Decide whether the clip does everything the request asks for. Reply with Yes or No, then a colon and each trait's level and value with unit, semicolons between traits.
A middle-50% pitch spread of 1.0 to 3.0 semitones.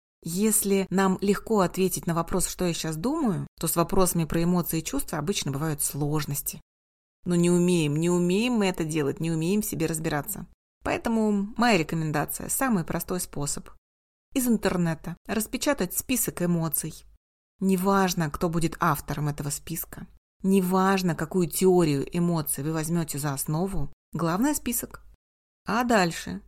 No: average, 3.5 semitones